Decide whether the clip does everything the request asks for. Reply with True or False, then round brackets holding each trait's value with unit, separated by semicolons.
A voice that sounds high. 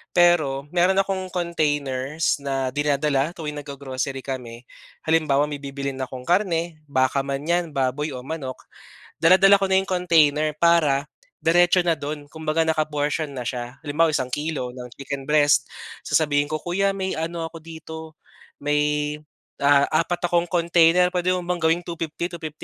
False (155 Hz)